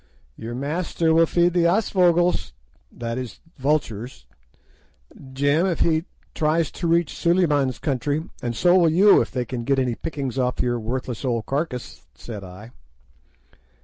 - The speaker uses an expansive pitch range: Yes, wide, 5.7 semitones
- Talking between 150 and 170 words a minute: No, average, 140 wpm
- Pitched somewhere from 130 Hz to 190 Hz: Yes, medium, 140 Hz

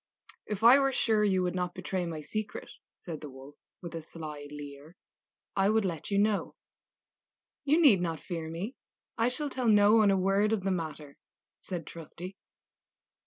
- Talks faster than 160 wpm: Yes, average, 175 wpm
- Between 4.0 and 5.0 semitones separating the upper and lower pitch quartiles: Yes, average, 4.7 semitones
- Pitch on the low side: No, medium, 185 Hz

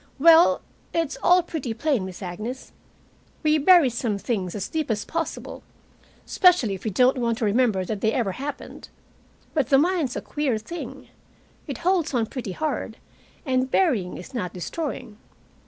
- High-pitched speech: Yes, very high, 255 Hz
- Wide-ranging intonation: Yes, wide, 6.4 semitones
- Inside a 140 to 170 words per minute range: Yes, average, 160 wpm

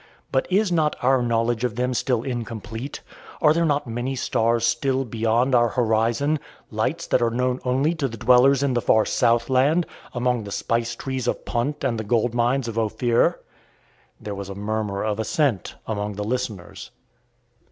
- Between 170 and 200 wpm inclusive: Yes, average, 175 wpm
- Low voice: Yes, low, 120 Hz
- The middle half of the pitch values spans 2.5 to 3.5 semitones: Yes, average, 2.8 semitones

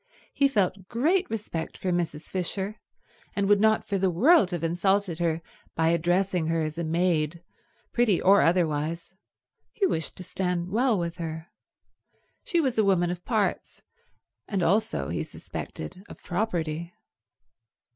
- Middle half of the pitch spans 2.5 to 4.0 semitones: Yes, average, 3.5 semitones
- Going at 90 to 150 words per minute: Yes, average, 145 wpm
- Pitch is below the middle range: No, medium, 180 Hz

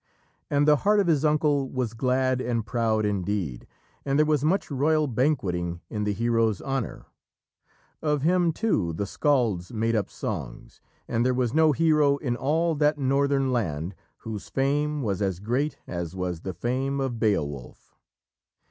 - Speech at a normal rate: Yes, average, 160 wpm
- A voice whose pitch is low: Yes, low, 130 Hz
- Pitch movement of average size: No, wide, 6.0 semitones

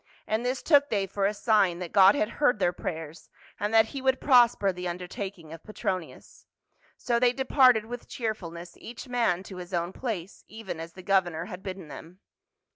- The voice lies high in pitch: Yes, high, 195 Hz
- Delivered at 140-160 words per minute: No, average, 190 wpm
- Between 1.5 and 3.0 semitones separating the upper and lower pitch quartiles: No, average, 5.1 semitones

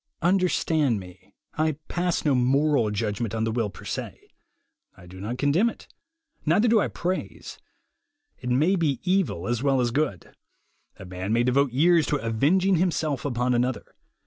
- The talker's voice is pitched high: No, low, 135 Hz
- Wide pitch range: Yes, wide, 6.5 semitones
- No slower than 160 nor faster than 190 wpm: Yes, average, 165 wpm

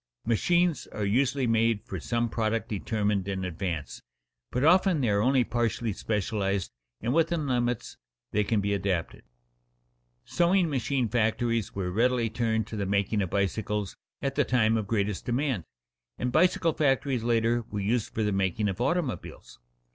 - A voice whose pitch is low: Yes, low, 115 Hz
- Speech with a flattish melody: No, average, 3.8 semitones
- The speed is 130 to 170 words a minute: Yes, average, 155 wpm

